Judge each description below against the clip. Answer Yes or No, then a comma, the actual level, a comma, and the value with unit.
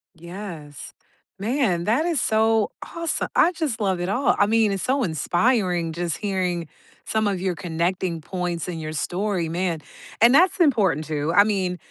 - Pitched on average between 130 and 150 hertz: No, high, 190 Hz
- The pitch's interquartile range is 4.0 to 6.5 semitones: Yes, average, 4.5 semitones